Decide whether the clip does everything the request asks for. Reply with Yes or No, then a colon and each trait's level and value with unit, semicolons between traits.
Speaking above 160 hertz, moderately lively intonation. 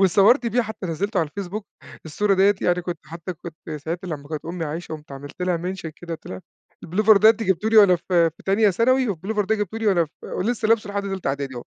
Yes: medium, 185 Hz; average, 4.0 semitones